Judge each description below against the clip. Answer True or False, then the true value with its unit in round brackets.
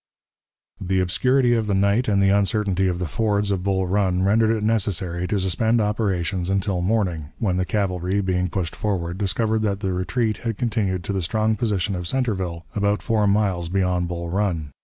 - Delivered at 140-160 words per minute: False (185 wpm)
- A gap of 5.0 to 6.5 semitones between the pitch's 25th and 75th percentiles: False (2.8 semitones)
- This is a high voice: False (100 Hz)